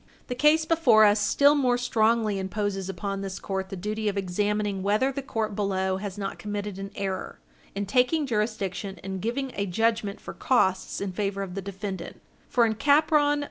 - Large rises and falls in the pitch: No, average, 3.3 semitones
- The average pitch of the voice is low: No, high, 205 Hz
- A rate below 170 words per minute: No, average, 185 wpm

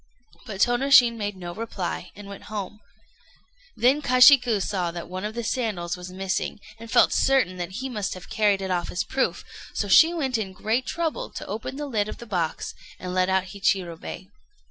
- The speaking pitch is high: Yes, high, 205 Hz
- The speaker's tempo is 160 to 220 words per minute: Yes, average, 190 wpm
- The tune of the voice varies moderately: Yes, average, 4.7 semitones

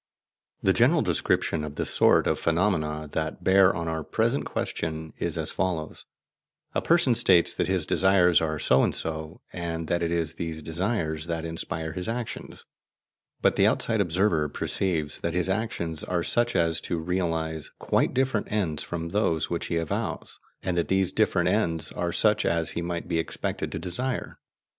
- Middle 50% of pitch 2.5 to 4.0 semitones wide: Yes, average, 2.9 semitones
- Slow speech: No, average, 175 wpm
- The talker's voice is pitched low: Yes, very low, 85 Hz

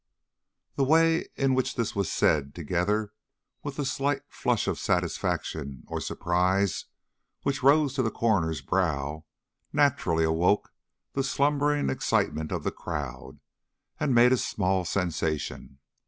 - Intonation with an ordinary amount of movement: No, wide, 9.0 semitones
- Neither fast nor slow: No, slow, 130 wpm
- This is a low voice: Yes, low, 100 Hz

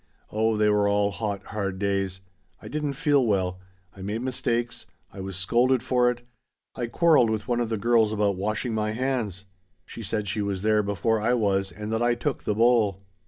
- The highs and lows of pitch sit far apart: No, average, 3.2 semitones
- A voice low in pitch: Yes, low, 110 Hz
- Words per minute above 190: Yes, average, 200 wpm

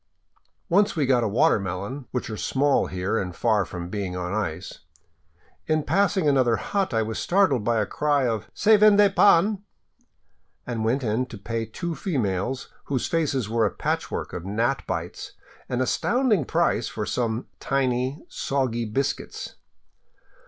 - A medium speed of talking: Yes, average, 155 wpm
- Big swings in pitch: Yes, wide, 6.0 semitones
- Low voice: Yes, low, 125 Hz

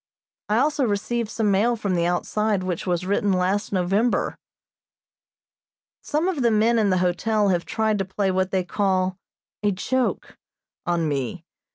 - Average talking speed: Yes, average, 160 wpm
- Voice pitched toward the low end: No, high, 200 Hz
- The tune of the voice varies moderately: Yes, average, 3.1 semitones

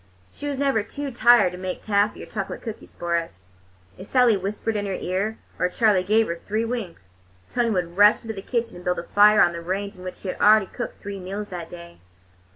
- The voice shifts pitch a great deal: No, average, 3.6 semitones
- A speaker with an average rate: No, fast, 230 wpm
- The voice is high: Yes, high, 200 Hz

